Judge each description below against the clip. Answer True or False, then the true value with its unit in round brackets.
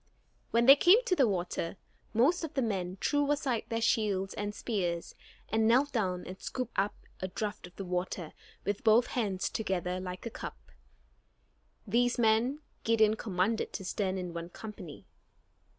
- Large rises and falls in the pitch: False (4.4 semitones)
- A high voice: True (215 Hz)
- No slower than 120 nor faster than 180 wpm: True (165 wpm)